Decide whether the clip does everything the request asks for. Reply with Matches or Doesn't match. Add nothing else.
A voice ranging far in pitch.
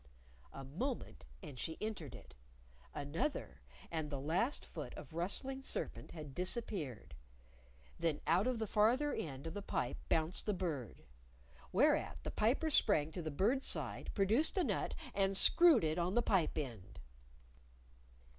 Matches